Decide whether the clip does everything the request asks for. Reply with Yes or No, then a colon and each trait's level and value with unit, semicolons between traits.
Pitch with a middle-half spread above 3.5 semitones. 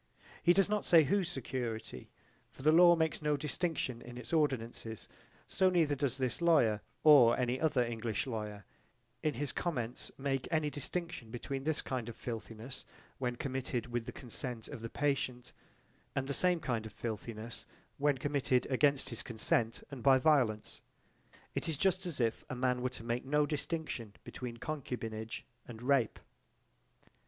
Yes: average, 4.1 semitones